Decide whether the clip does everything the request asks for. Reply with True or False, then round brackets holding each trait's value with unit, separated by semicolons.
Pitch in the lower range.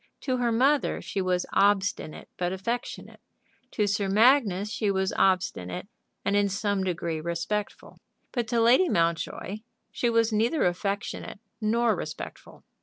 False (205 Hz)